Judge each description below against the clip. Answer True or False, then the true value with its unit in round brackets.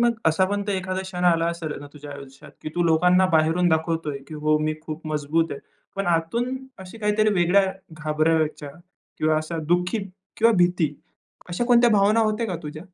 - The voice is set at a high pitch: False (170 Hz)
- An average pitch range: True (3.7 semitones)